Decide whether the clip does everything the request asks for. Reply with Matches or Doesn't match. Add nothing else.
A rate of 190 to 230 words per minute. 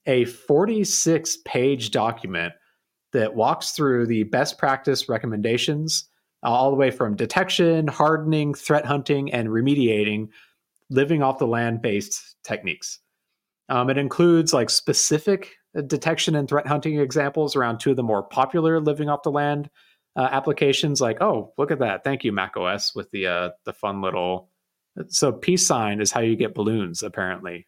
Doesn't match